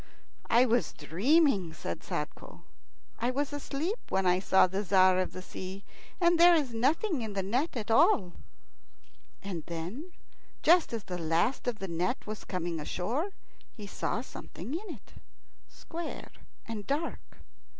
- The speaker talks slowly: No, average, 150 wpm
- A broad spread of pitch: Yes, wide, 7.8 semitones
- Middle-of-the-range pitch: No, high, 225 Hz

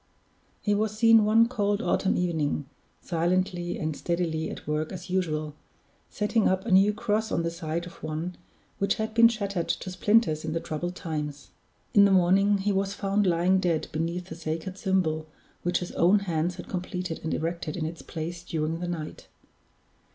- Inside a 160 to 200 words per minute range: Yes, average, 180 wpm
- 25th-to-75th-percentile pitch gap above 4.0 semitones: No, average, 3.5 semitones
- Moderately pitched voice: Yes, medium, 180 Hz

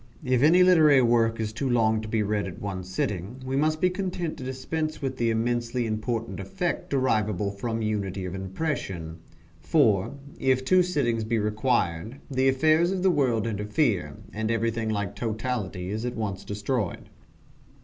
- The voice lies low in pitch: Yes, low, 115 Hz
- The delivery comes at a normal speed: Yes, average, 165 wpm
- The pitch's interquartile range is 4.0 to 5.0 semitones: Yes, average, 4.3 semitones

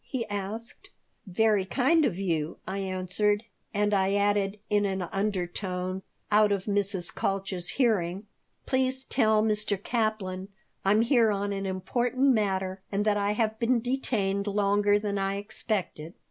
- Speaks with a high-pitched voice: Yes, high, 205 Hz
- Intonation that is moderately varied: No, narrow, 2.2 semitones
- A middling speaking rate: Yes, average, 145 wpm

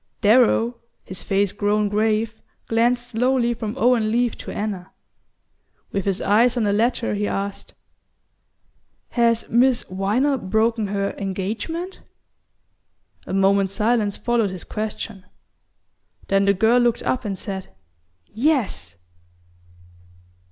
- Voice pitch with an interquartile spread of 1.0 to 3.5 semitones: Yes, average, 3.2 semitones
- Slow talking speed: Yes, slow, 115 wpm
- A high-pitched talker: Yes, high, 215 Hz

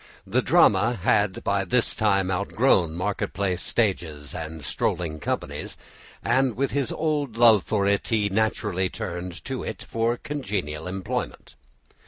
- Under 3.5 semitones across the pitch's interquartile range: No, average, 4.2 semitones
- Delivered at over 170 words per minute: No, average, 145 wpm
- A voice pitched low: Yes, low, 100 Hz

